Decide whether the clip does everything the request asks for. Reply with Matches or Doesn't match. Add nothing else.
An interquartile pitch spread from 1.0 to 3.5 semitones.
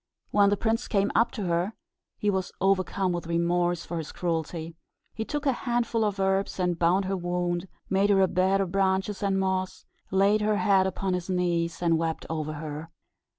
Matches